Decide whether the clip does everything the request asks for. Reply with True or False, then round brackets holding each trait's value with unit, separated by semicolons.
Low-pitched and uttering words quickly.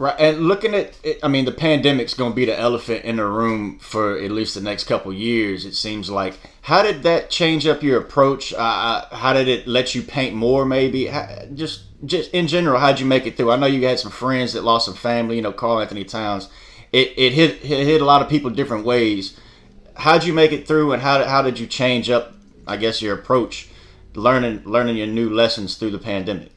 True (120 Hz; 235 wpm)